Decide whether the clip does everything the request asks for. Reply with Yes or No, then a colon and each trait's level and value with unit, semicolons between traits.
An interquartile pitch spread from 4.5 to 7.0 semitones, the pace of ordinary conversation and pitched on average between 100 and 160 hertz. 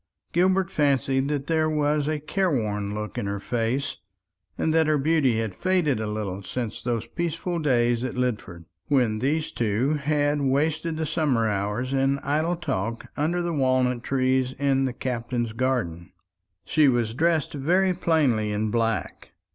Yes: average, 5.1 semitones; average, 155 wpm; low, 135 Hz